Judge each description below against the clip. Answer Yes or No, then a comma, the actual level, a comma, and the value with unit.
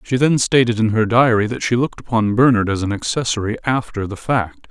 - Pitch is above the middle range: No, low, 115 Hz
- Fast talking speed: Yes, fast, 215 wpm